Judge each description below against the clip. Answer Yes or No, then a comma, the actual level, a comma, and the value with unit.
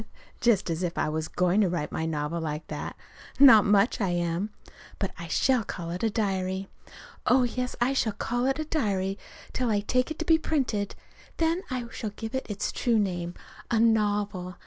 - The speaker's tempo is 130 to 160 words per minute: No, average, 195 wpm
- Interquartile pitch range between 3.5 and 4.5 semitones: No, wide, 5.4 semitones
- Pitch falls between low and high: No, high, 205 Hz